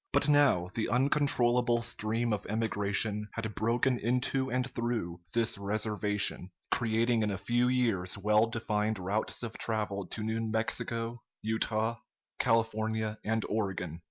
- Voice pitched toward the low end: Yes, low, 110 Hz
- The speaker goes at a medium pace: No, slow, 130 wpm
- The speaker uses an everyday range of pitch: No, narrow, 2.0 semitones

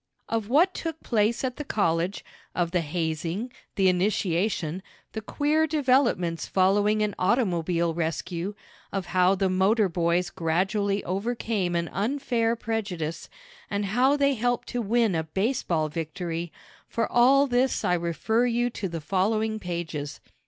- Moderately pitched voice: No, high, 195 Hz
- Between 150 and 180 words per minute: No, average, 140 wpm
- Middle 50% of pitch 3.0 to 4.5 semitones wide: No, wide, 5.4 semitones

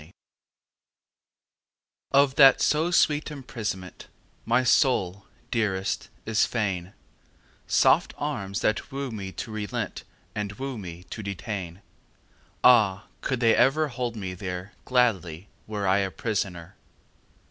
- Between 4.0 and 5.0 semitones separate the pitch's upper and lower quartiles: Yes, average, 4.7 semitones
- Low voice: Yes, low, 105 Hz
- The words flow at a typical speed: No, slow, 120 wpm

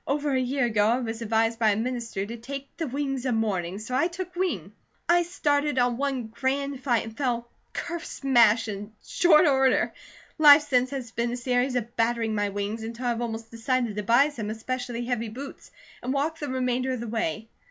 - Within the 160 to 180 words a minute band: No, fast, 205 wpm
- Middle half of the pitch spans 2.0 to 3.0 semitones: No, average, 3.4 semitones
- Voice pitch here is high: Yes, high, 245 Hz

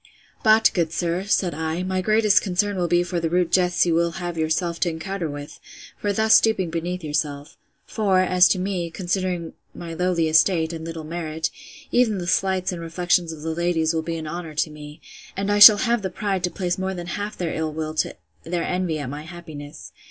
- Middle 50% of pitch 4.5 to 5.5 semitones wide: No, narrow, 2.6 semitones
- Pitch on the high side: No, medium, 175 Hz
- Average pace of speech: No, fast, 210 wpm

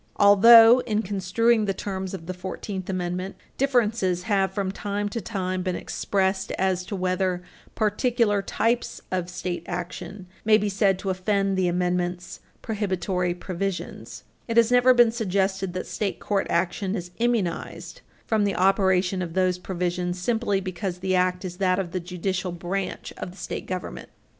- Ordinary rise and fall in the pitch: No, narrow, 2.2 semitones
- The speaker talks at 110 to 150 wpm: No, average, 160 wpm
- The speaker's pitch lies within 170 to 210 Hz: Yes, high, 190 Hz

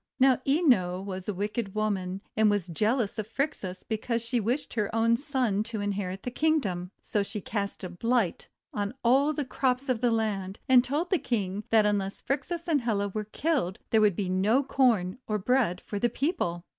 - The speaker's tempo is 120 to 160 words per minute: No, average, 195 wpm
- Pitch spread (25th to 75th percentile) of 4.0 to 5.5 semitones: Yes, average, 4.4 semitones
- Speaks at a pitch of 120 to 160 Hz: No, high, 215 Hz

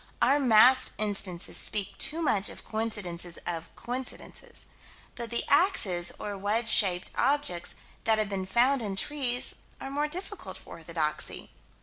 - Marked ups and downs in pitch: Yes, wide, 5.7 semitones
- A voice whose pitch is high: Yes, high, 220 Hz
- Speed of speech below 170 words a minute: Yes, average, 140 wpm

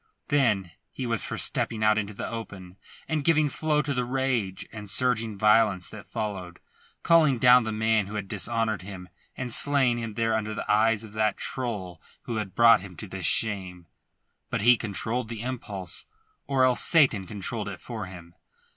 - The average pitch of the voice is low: Yes, low, 110 Hz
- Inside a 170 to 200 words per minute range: Yes, average, 180 wpm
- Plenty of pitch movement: No, average, 3.7 semitones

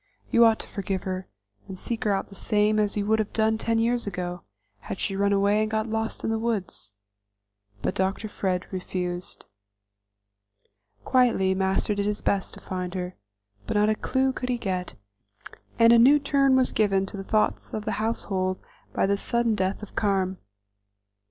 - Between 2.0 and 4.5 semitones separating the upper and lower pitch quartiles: Yes, average, 2.8 semitones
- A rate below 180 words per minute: No, average, 185 wpm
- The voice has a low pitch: No, high, 205 Hz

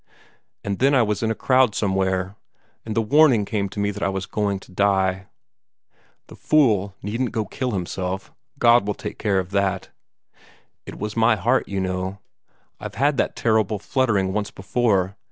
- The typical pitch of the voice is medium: No, low, 100 Hz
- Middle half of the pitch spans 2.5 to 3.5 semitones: Yes, average, 2.9 semitones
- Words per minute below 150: No, average, 175 wpm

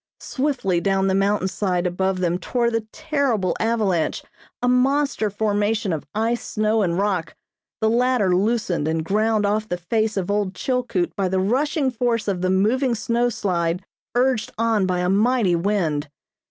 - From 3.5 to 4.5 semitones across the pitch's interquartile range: Yes, average, 4.1 semitones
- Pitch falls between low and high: No, high, 210 Hz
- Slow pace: No, average, 160 wpm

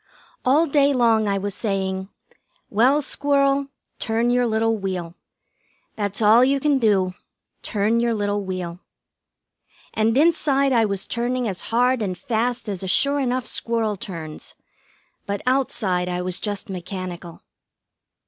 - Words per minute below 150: Yes, average, 140 wpm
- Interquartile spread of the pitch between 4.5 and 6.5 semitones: Yes, average, 4.8 semitones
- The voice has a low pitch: No, high, 220 Hz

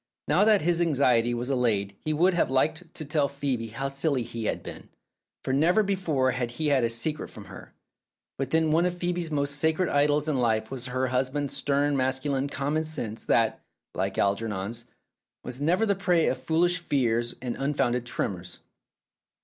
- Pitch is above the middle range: No, medium, 140 Hz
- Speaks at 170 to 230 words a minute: Yes, average, 180 wpm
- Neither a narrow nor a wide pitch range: Yes, average, 4.6 semitones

